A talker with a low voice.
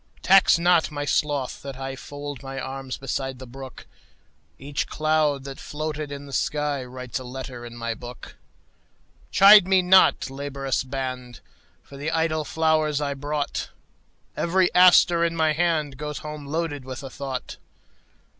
No: medium, 145 Hz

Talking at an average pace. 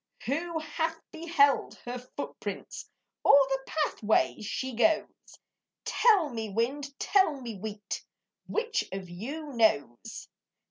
No: slow, 110 wpm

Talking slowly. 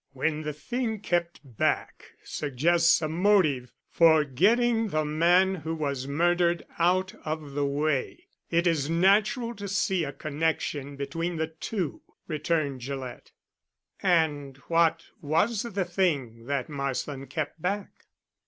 Yes: slow, 130 wpm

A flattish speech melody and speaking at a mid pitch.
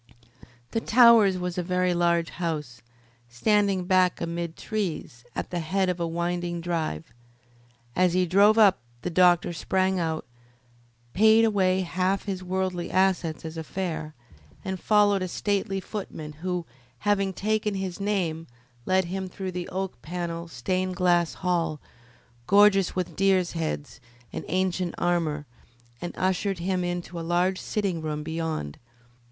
Yes: narrow, 2.2 semitones; medium, 180 Hz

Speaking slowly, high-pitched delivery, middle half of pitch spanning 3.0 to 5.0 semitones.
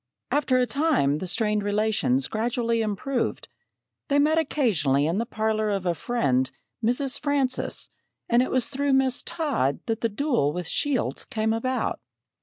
No: average, 155 wpm; high, 235 Hz; average, 4.5 semitones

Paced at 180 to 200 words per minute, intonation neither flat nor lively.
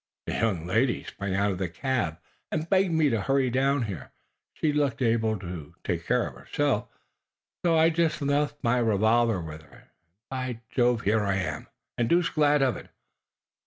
No: average, 185 wpm; wide, 6.2 semitones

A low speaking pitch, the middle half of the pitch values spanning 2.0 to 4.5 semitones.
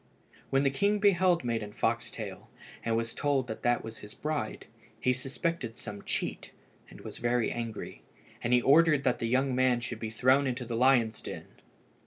Yes: low, 125 Hz; average, 3.2 semitones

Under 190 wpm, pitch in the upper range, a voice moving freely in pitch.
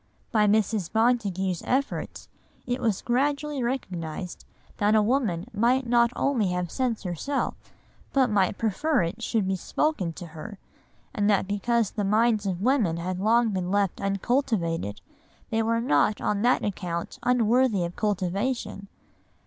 No: average, 145 wpm; high, 210 Hz; average, 4.5 semitones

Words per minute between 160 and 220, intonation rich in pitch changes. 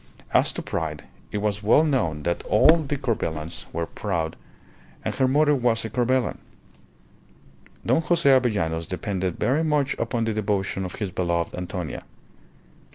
No: average, 150 wpm; wide, 7.0 semitones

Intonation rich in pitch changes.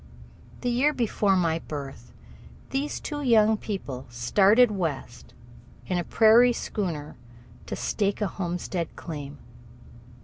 Yes: wide, 6.2 semitones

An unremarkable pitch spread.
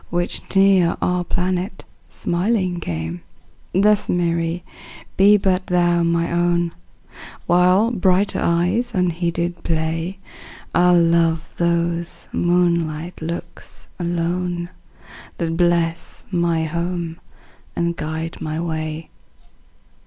No: narrow, 1.2 semitones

